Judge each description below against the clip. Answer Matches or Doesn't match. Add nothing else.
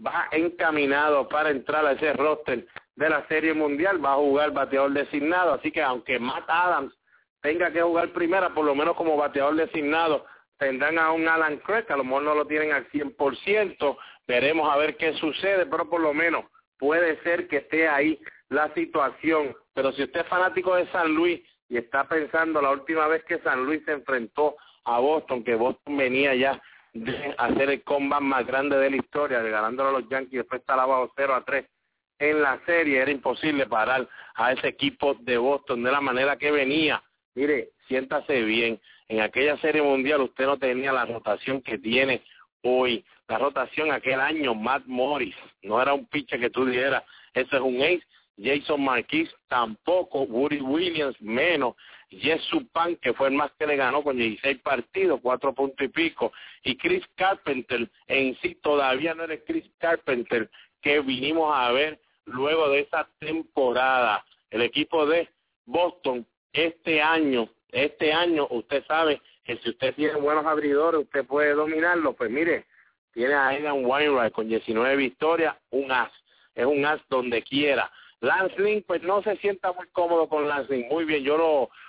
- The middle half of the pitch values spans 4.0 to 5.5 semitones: Doesn't match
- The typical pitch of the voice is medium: Matches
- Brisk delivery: Doesn't match